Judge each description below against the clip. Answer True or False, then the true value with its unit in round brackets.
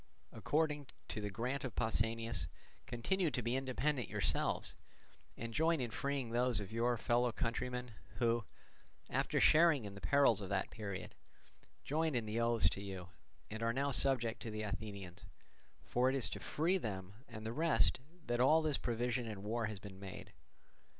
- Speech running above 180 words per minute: False (170 wpm)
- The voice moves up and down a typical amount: True (3.8 semitones)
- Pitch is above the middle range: False (120 Hz)